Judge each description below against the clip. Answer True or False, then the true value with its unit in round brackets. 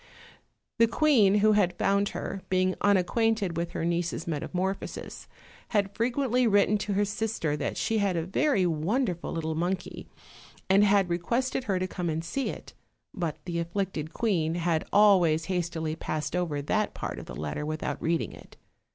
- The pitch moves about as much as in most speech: True (3.8 semitones)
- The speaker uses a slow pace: False (175 wpm)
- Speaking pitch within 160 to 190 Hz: True (185 Hz)